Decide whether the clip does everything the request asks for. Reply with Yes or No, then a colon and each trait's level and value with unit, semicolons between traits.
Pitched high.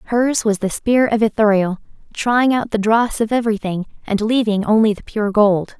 Yes: high, 215 Hz